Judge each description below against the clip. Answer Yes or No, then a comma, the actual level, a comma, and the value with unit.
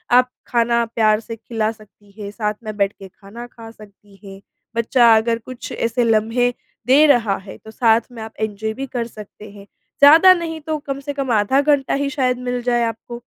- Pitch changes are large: No, average, 2.9 semitones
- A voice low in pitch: No, high, 230 Hz